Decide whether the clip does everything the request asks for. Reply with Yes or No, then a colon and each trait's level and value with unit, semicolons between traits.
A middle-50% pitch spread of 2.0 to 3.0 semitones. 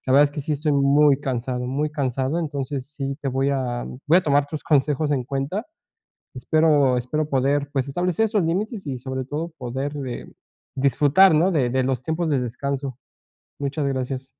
Yes: narrow, 2.5 semitones